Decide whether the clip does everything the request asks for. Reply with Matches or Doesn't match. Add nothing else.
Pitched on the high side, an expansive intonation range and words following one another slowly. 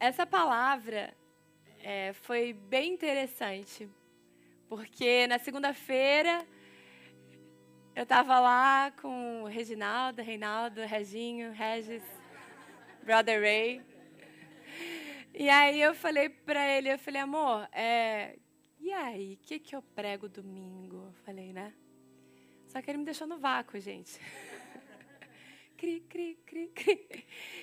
Matches